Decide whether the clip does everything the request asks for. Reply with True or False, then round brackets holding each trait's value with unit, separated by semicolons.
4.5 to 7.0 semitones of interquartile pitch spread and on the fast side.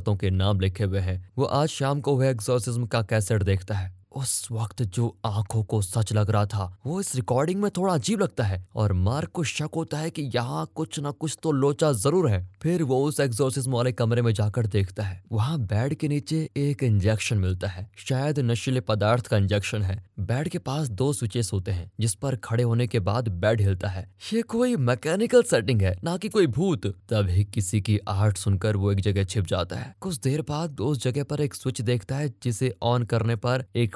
True (5.4 semitones; 215 wpm)